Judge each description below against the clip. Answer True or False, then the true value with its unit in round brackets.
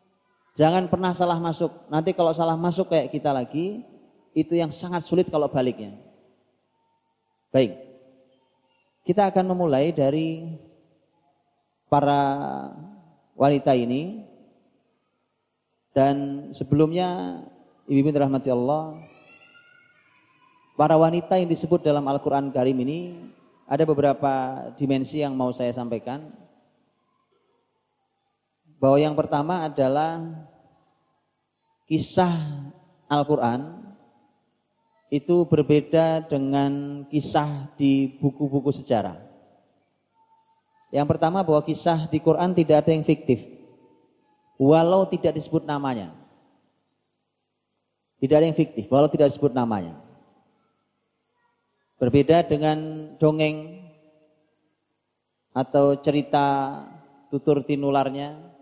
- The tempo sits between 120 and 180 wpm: False (90 wpm)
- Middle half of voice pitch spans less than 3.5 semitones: True (3.0 semitones)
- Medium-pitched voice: True (150 Hz)